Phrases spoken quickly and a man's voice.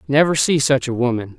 Yes: fast, 260 wpm; male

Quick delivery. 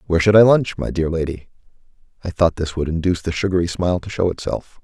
Yes: fast, 225 wpm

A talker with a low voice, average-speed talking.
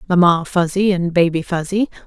No: medium, 180 Hz; average, 145 wpm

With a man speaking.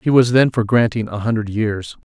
Yes: male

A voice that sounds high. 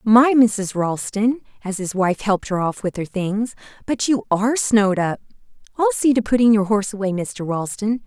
Yes: high, 210 Hz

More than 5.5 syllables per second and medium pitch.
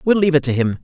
Yes: 8.3 syllables/s; medium, 155 Hz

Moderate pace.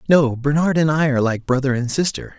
No: fast, 225 wpm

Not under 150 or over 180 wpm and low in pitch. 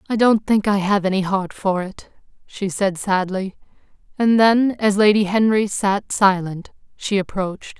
No: average, 160 wpm; high, 200 Hz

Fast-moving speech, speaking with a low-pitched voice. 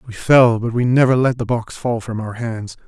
Yes: fast, 250 wpm; low, 115 Hz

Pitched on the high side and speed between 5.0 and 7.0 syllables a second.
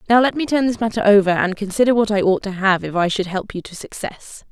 Yes: high, 205 Hz; 6.1 syllables/s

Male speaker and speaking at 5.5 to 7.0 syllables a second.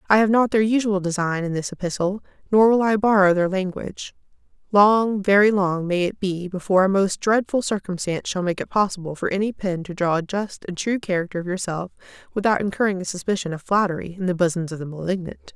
No: female; 6.0 syllables/s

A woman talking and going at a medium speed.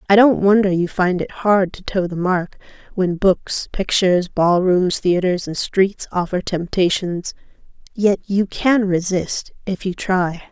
Yes: female; average, 160 wpm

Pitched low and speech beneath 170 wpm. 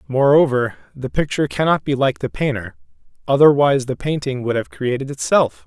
Yes: low, 130 Hz; average, 160 wpm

